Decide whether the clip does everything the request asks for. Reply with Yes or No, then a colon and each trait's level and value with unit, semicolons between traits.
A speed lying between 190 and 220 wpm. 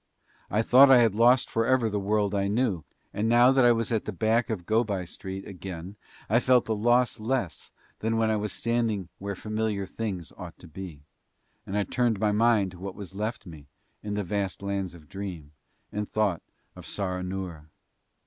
Yes: average, 195 wpm